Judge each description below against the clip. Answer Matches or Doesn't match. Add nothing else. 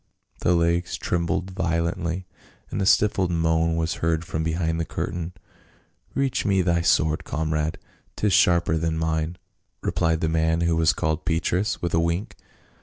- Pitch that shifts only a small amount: Matches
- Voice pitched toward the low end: Matches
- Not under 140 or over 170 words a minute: Matches